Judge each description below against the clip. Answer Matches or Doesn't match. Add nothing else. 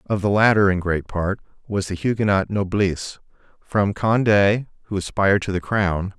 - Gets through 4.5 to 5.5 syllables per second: Matches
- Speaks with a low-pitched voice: Matches